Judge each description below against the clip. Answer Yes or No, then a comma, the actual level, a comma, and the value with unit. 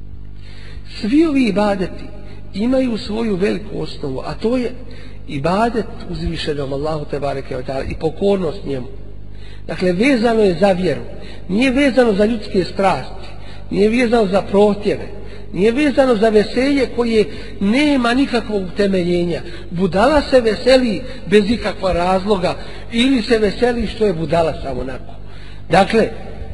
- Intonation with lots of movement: Yes, wide, 8.8 semitones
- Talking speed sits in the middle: No, slow, 120 wpm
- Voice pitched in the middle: No, high, 195 Hz